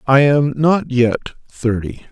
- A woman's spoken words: No, male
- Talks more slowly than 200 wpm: Yes, average, 140 wpm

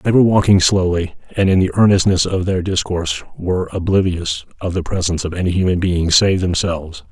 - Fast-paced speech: No, average, 185 wpm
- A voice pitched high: No, very low, 90 Hz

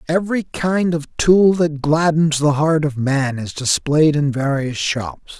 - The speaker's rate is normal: Yes, average, 165 wpm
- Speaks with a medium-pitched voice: Yes, medium, 150 Hz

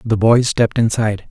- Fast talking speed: No, average, 185 wpm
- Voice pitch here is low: Yes, low, 110 Hz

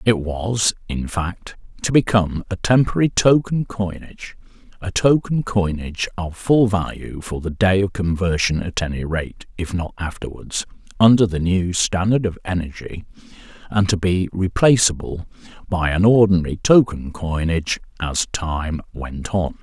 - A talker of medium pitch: No, very low, 95 Hz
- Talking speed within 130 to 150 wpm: Yes, average, 140 wpm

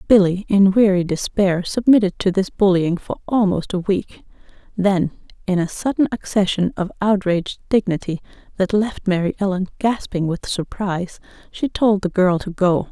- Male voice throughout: No, female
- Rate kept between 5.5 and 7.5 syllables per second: No, 4.9 syllables/s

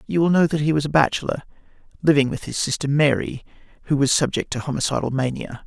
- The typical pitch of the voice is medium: Yes, medium, 145 Hz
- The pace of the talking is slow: No, average, 200 wpm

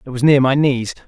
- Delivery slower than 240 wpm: No, fast, 280 wpm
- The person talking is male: Yes, male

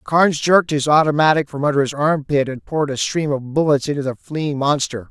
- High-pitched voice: No, medium, 145 Hz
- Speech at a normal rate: No, fast, 210 wpm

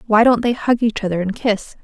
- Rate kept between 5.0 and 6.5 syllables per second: Yes, 5.5 syllables/s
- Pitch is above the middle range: Yes, high, 220 Hz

